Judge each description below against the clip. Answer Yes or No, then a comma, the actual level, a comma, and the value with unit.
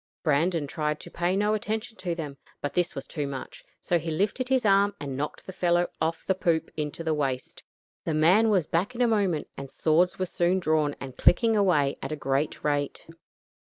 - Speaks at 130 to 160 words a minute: No, fast, 205 wpm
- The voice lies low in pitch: No, medium, 165 Hz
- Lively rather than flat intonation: No, average, 4.5 semitones